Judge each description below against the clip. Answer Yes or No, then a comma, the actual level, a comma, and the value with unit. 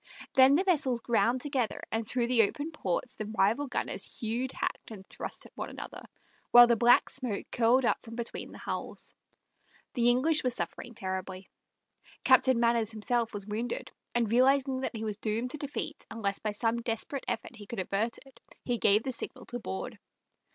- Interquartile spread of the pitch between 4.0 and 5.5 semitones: No, average, 2.9 semitones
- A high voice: Yes, high, 235 Hz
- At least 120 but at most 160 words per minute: No, average, 185 wpm